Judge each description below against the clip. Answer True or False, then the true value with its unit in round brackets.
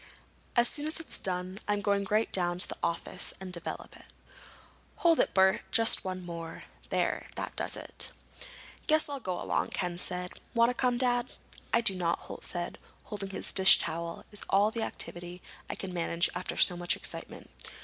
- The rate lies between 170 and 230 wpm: True (185 wpm)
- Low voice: False (190 Hz)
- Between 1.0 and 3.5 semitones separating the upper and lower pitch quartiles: False (4.6 semitones)